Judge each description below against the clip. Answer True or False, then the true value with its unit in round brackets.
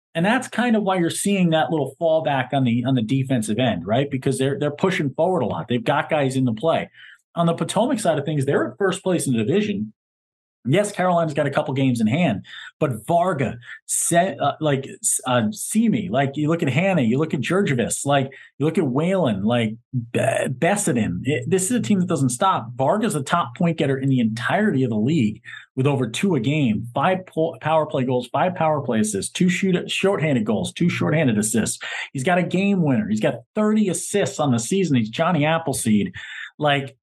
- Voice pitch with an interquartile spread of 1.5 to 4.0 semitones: False (5.6 semitones)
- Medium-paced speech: False (215 wpm)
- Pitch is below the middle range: False (155 Hz)